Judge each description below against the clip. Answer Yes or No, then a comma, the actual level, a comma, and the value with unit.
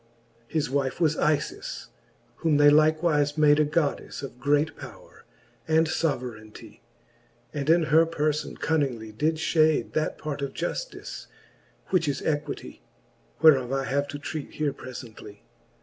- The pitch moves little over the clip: Yes, narrow, 2.3 semitones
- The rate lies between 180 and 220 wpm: No, slow, 135 wpm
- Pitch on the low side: No, medium, 150 Hz